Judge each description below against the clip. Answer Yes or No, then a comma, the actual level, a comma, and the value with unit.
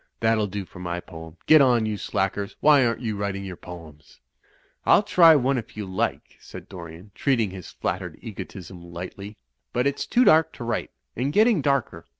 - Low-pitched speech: Yes, low, 105 Hz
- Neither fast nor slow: Yes, average, 180 wpm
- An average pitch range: No, wide, 6.6 semitones